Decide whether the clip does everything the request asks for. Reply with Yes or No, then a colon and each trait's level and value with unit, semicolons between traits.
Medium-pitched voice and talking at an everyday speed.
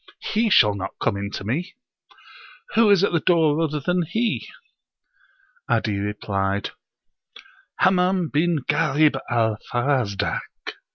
No: medium, 150 Hz; slow, 120 wpm